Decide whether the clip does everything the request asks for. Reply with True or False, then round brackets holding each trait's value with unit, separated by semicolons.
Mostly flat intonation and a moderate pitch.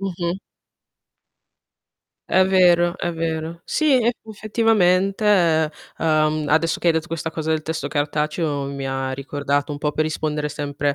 False (3.1 semitones; 160 Hz)